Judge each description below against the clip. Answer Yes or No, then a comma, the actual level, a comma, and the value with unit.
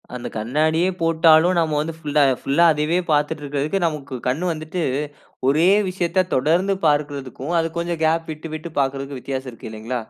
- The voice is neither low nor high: Yes, medium, 155 Hz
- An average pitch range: Yes, average, 3.1 semitones